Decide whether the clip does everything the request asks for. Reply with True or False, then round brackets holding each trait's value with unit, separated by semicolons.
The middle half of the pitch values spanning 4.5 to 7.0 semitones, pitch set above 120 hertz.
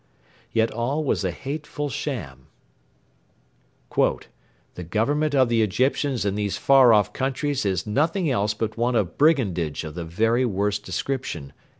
False (5.6 semitones; 115 Hz)